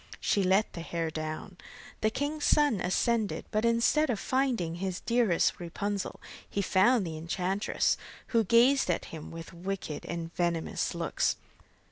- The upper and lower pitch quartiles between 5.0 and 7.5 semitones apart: Yes, wide, 5.4 semitones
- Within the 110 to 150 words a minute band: Yes, average, 145 wpm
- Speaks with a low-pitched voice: No, high, 195 Hz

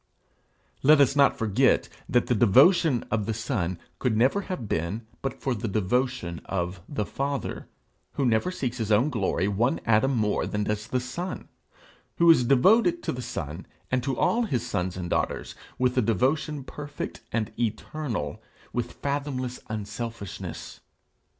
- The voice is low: Yes, low, 120 Hz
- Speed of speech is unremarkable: Yes, average, 155 wpm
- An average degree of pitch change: Yes, average, 4.6 semitones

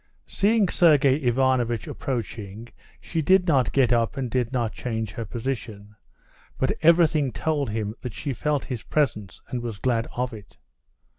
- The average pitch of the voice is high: No, low, 125 Hz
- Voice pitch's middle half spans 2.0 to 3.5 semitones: No, average, 3.9 semitones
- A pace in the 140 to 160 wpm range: Yes, average, 155 wpm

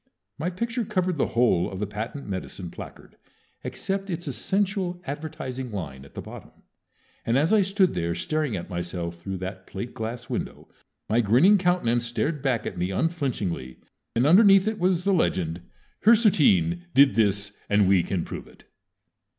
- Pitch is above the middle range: No, low, 125 Hz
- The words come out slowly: No, average, 165 wpm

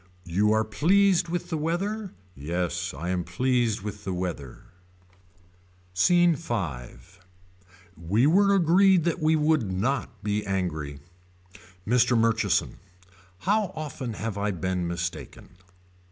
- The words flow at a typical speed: No, slow, 120 wpm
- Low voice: Yes, low, 110 Hz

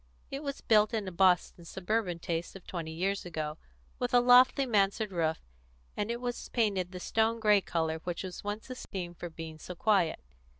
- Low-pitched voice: No, high, 190 Hz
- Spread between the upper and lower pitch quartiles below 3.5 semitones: No, average, 4.5 semitones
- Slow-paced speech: No, average, 185 wpm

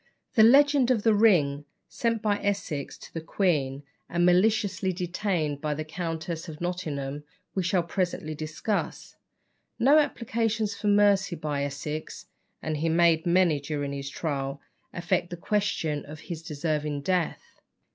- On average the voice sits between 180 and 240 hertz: No, medium, 170 Hz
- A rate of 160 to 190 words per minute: No, average, 145 wpm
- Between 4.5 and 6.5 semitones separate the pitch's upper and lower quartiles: Yes, average, 5.1 semitones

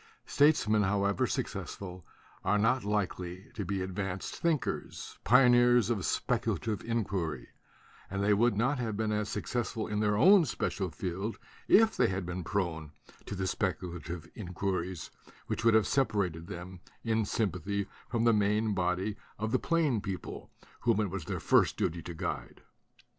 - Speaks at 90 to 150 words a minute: No, average, 160 wpm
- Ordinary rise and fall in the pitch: Yes, average, 3.6 semitones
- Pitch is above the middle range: No, low, 100 Hz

